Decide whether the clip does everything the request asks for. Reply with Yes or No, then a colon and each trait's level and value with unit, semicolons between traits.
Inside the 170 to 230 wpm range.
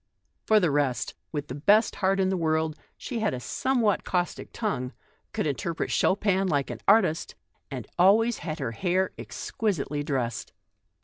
No: average, 160 wpm